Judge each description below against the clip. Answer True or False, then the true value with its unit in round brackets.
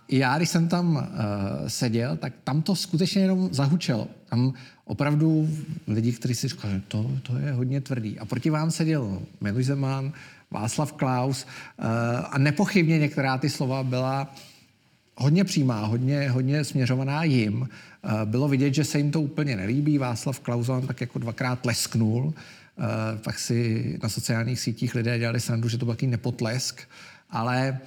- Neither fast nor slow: True (160 wpm)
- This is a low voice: True (130 Hz)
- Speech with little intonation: False (3.8 semitones)